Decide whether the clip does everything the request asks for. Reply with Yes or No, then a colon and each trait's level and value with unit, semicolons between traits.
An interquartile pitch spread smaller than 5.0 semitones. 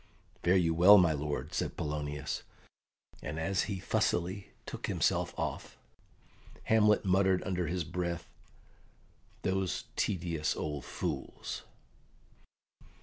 Yes: average, 3.3 semitones